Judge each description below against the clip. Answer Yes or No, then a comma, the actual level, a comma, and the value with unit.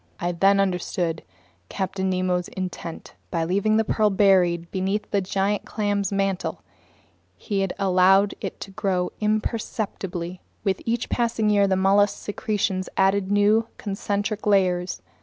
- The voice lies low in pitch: No, high, 195 Hz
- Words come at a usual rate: No, slow, 130 wpm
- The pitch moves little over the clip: Yes, narrow, 1.9 semitones